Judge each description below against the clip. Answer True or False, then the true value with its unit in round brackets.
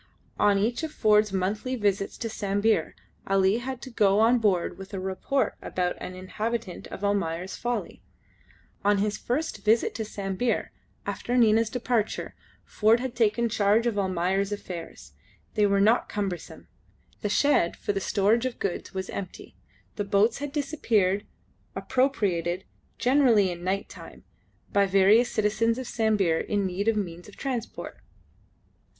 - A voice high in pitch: True (210 Hz)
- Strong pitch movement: False (3.3 semitones)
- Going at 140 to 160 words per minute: True (150 wpm)